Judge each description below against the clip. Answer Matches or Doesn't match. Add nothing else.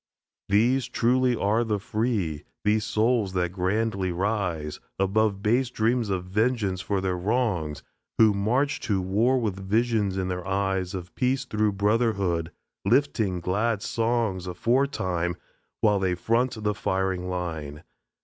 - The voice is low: Matches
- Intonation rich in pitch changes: Doesn't match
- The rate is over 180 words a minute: Doesn't match